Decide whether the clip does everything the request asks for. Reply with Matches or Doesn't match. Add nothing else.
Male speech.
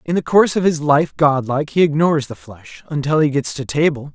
Matches